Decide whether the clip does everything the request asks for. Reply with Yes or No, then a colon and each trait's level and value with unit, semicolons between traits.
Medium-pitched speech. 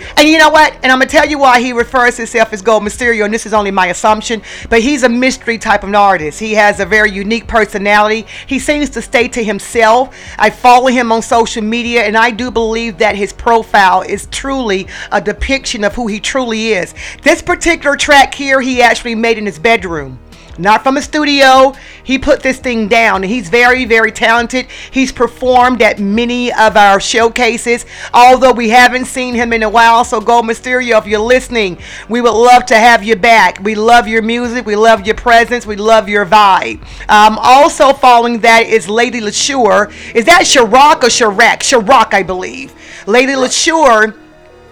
No: high, 235 Hz